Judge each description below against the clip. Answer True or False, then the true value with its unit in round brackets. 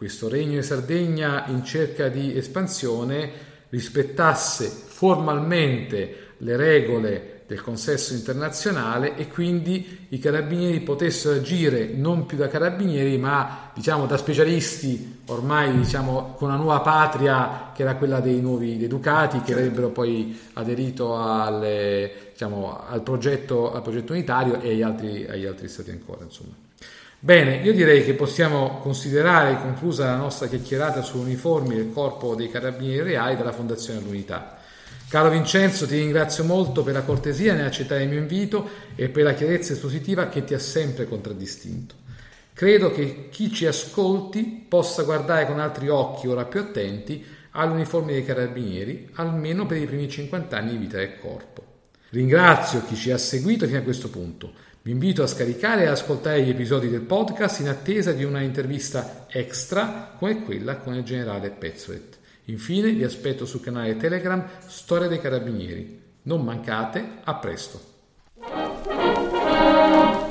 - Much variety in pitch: False (4.6 semitones)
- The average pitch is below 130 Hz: False (140 Hz)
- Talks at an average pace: True (145 wpm)